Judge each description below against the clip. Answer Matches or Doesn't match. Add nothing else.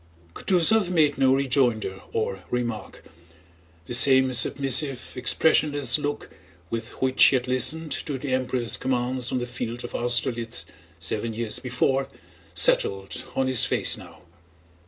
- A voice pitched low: Matches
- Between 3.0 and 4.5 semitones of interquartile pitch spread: Doesn't match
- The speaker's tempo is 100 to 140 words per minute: Matches